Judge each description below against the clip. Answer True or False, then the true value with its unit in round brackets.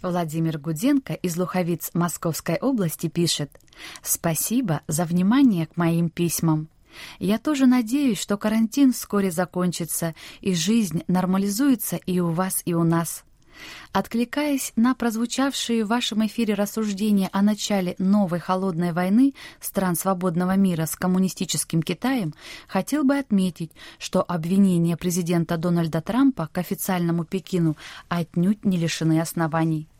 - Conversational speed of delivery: True (125 wpm)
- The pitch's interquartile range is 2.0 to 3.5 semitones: False (4.0 semitones)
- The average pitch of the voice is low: False (185 Hz)